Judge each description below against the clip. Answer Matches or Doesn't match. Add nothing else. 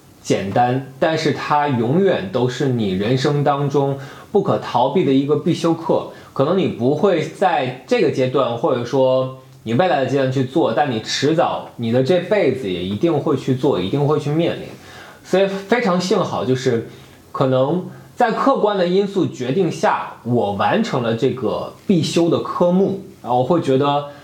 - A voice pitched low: Doesn't match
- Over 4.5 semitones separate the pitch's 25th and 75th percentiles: Matches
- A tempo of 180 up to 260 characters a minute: Matches